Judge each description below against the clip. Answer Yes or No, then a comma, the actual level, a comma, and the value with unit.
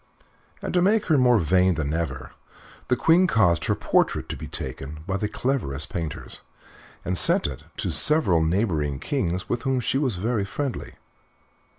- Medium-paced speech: Yes, average, 170 wpm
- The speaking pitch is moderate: No, very low, 95 Hz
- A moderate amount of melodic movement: No, wide, 8.4 semitones